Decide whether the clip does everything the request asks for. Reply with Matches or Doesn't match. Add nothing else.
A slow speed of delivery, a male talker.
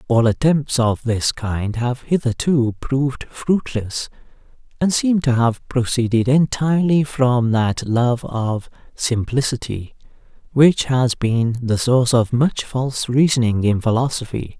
Matches